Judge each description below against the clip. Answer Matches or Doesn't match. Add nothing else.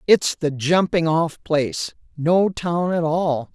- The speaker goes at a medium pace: Matches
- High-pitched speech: Doesn't match